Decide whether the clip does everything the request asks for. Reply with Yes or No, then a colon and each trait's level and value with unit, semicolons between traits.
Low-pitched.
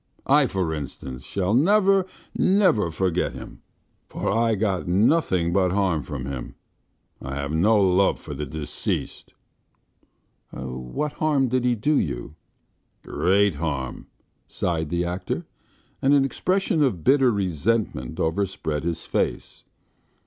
Yes: very low, 95 Hz